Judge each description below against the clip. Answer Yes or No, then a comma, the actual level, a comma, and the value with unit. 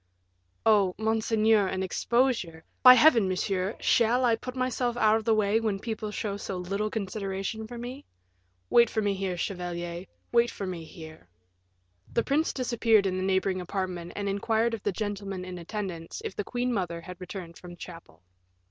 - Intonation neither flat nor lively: Yes, average, 3.6 semitones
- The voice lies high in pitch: Yes, high, 200 Hz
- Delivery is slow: No, average, 175 wpm